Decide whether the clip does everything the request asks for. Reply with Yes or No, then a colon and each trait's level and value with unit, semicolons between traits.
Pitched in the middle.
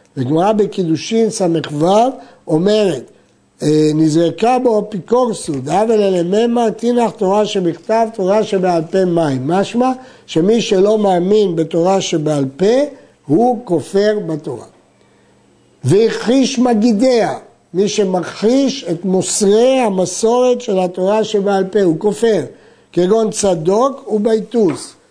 No: high, 200 Hz